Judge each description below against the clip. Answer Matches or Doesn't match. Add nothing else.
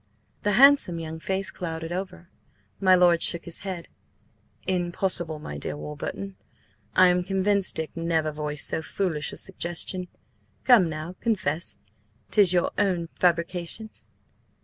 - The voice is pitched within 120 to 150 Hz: Doesn't match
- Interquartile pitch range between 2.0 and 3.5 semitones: Matches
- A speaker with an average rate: Doesn't match